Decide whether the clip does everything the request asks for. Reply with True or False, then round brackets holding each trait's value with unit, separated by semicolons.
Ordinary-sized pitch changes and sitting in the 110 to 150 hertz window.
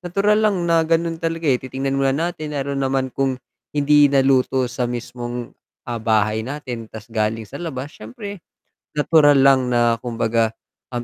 True (3.9 semitones; 135 Hz)